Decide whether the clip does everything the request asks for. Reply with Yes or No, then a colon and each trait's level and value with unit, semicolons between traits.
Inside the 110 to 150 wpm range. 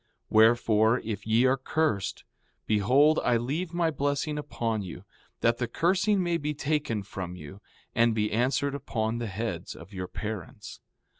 No: average, 160 wpm